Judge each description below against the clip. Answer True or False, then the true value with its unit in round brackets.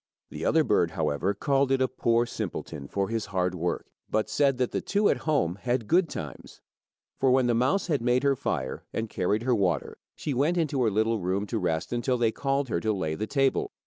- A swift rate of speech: True (220 wpm)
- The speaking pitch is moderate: False (115 Hz)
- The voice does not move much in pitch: False (5.6 semitones)